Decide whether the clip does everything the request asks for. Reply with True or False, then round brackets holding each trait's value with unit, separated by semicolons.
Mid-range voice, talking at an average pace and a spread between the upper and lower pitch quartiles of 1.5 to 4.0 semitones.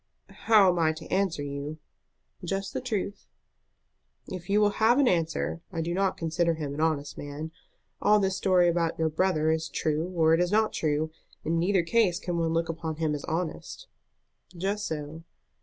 True (165 Hz; 180 wpm; 3.3 semitones)